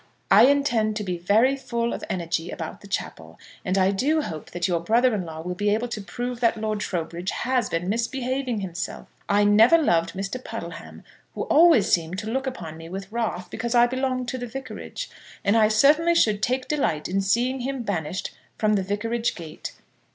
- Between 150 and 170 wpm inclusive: No, average, 195 wpm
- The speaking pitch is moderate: No, high, 215 Hz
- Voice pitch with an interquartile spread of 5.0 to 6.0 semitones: Yes, average, 5.3 semitones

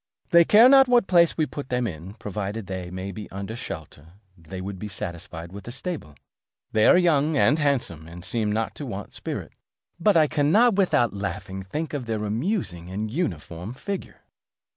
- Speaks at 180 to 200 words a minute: Yes, average, 185 wpm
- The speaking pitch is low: Yes, low, 110 Hz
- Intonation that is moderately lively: No, wide, 8.6 semitones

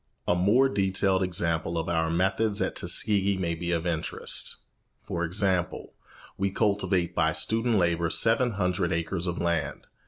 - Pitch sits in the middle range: No, very low, 90 Hz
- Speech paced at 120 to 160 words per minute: Yes, average, 150 wpm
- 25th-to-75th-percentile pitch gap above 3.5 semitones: No, average, 2.9 semitones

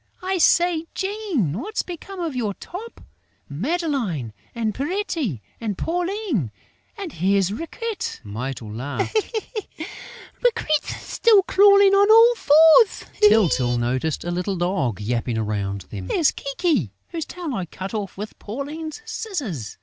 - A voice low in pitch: No, very high, 265 Hz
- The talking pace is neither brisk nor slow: No, slow, 125 wpm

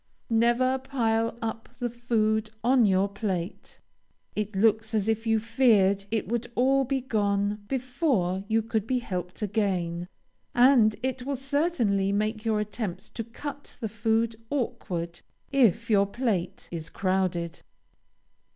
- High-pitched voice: Yes, high, 220 Hz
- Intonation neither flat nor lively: Yes, average, 3.4 semitones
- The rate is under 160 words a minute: Yes, slow, 135 wpm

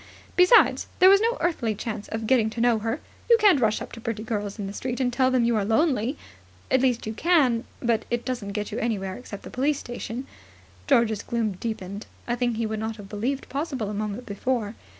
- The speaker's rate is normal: No, fast, 220 wpm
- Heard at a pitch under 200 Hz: No, high, 230 Hz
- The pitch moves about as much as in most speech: Yes, average, 3.3 semitones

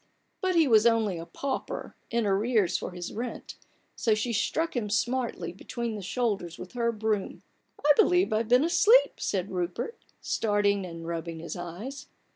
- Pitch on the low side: No, high, 215 Hz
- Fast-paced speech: No, average, 170 wpm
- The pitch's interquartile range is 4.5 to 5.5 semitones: Yes, average, 5.1 semitones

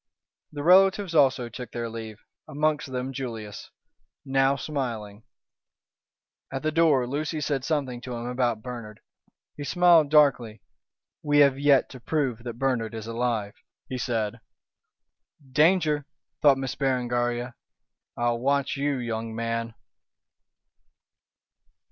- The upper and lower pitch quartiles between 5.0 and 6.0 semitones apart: No, average, 3.7 semitones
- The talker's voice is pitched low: Yes, low, 130 Hz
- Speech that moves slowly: Yes, slow, 120 wpm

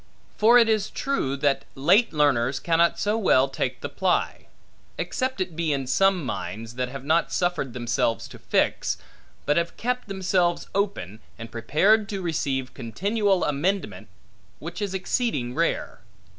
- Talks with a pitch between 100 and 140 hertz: No, medium, 170 Hz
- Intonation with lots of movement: Yes, wide, 6.9 semitones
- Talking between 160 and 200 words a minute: No, average, 150 wpm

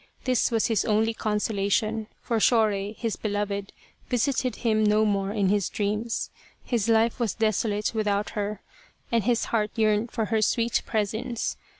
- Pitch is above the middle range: Yes, high, 215 Hz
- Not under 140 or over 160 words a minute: Yes, average, 155 wpm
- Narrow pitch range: Yes, narrow, 1.7 semitones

